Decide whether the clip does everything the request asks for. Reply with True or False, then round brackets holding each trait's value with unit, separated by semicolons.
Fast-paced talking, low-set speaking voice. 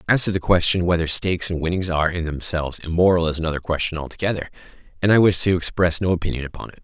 True (220 wpm; 85 Hz)